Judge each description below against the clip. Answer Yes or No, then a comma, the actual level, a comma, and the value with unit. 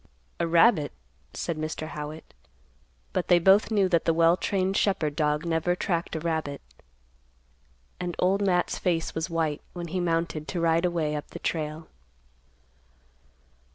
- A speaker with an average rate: Yes, average, 150 wpm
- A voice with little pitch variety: Yes, narrow, 2.3 semitones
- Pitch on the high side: No, medium, 165 Hz